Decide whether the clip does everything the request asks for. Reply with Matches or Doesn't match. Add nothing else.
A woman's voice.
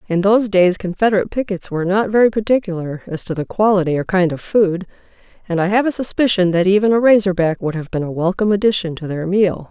Matches